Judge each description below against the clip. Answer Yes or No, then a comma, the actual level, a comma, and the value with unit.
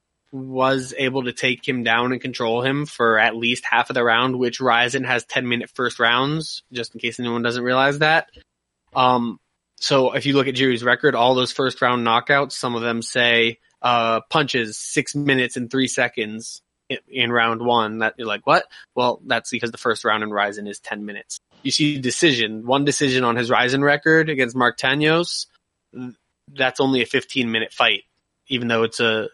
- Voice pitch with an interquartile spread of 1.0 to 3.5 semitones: Yes, narrow, 2.6 semitones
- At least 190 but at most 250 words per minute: Yes, average, 195 wpm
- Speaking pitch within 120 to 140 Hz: Yes, low, 125 Hz